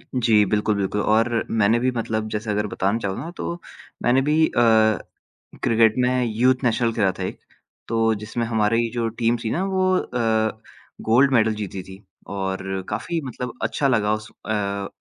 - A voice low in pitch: Yes, low, 110 Hz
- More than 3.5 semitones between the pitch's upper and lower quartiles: No, average, 2.7 semitones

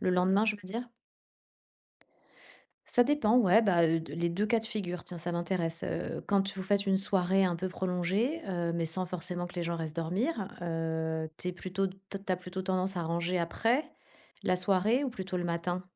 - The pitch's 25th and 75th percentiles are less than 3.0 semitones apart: Yes, narrow, 2.5 semitones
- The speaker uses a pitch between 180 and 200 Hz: Yes, medium, 185 Hz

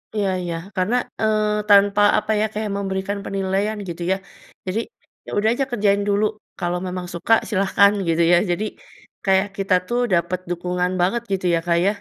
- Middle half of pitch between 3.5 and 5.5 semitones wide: No, average, 2.7 semitones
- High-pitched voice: Yes, high, 195 Hz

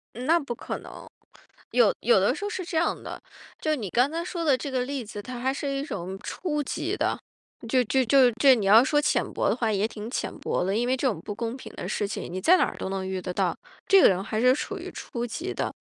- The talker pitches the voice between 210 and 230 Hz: No, very high, 250 Hz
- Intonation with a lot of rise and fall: Yes, wide, 6.0 semitones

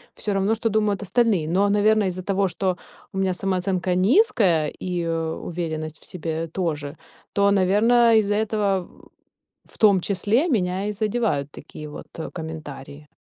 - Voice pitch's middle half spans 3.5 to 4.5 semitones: Yes, average, 4.0 semitones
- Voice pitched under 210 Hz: Yes, high, 190 Hz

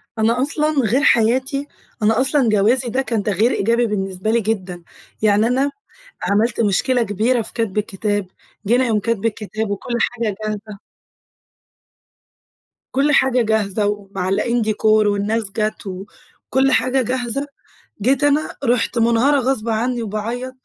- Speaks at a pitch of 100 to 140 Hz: No, high, 225 Hz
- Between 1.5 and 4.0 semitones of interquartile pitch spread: Yes, average, 3.4 semitones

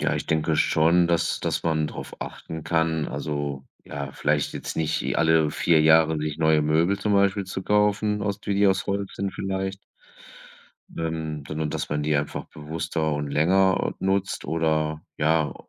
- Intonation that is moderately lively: Yes, average, 3.8 semitones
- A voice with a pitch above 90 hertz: No, very low, 80 Hz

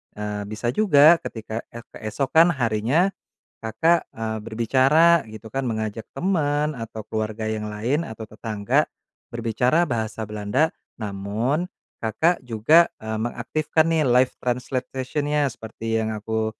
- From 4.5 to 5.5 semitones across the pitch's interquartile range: Yes, average, 5.1 semitones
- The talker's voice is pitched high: No, low, 115 Hz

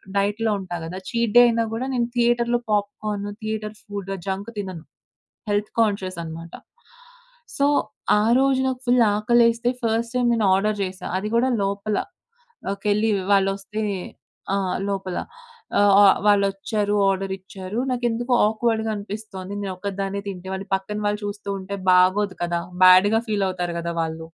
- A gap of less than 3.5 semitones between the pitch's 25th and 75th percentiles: Yes, average, 2.8 semitones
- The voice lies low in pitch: No, high, 205 Hz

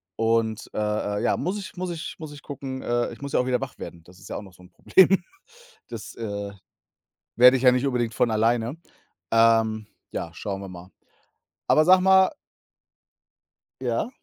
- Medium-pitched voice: No, low, 120 Hz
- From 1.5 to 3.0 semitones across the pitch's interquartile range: No, average, 4.7 semitones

